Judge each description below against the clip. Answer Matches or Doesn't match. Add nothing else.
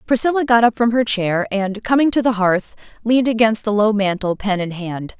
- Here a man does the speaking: Doesn't match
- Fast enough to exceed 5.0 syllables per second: Matches